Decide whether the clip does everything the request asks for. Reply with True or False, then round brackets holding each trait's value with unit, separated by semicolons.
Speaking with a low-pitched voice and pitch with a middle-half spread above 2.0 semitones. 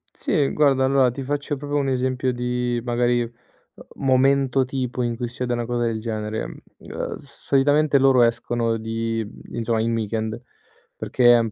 True (125 Hz; 2.6 semitones)